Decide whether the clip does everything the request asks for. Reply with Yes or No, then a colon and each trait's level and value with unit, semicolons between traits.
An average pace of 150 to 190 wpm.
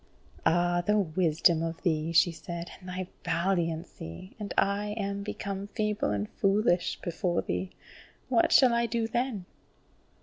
No: average, 140 wpm